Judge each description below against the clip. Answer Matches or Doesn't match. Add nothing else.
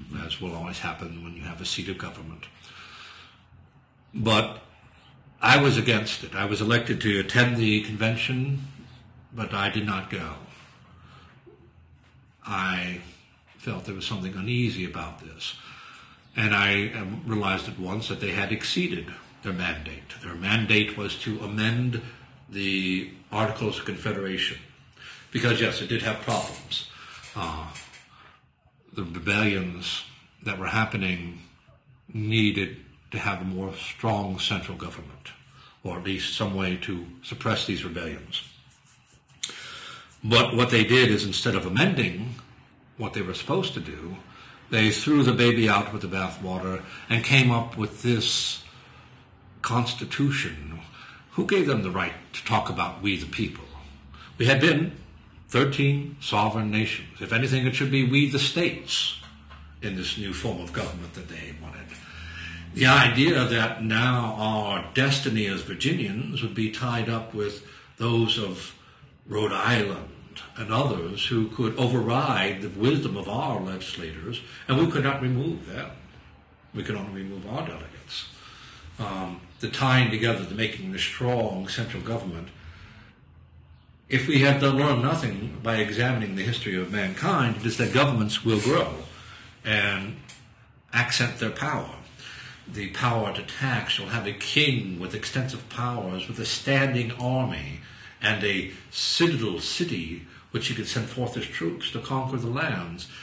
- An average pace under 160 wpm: Matches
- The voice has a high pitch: Doesn't match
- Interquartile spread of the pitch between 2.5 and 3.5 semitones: Doesn't match